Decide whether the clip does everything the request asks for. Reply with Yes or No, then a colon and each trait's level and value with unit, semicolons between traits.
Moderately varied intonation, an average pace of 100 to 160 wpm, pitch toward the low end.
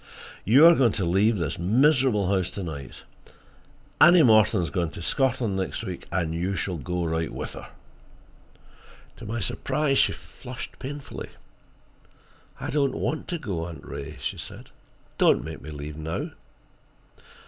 No: wide, 7.5 semitones; average, 155 wpm; low, 100 Hz